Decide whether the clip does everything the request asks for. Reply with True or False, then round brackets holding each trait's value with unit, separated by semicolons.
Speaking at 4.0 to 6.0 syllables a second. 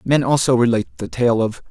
False (6.2 syllables/s)